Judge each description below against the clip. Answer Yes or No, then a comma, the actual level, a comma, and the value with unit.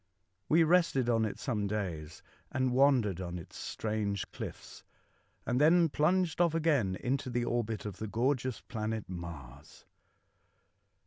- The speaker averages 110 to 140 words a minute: Yes, slow, 135 wpm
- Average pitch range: No, wide, 5.9 semitones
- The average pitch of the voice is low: Yes, low, 115 Hz